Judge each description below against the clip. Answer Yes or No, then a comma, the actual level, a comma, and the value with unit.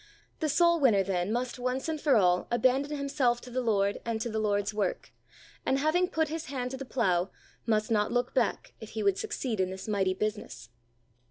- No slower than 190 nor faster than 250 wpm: Yes, fast, 205 wpm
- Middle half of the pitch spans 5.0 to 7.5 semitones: Yes, average, 5.3 semitones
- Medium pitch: No, high, 240 Hz